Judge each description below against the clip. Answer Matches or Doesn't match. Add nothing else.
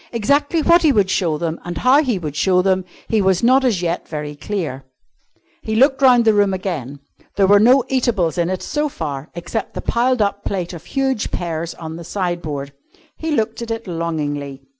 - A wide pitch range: Matches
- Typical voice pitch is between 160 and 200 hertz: Matches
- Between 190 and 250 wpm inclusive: Matches